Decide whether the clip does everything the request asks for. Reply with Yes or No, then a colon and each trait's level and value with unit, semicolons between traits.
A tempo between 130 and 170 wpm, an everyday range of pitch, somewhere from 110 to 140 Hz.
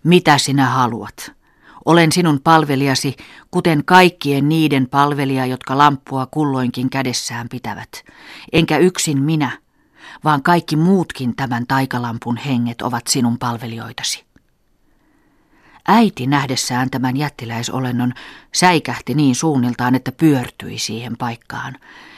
No: average, 105 wpm; average, 3.7 semitones; low, 135 Hz